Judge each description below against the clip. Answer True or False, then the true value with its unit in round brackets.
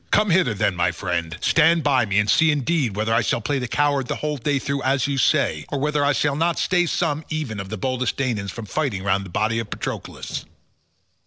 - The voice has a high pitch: False (130 Hz)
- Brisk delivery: True (230 wpm)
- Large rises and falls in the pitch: True (6.0 semitones)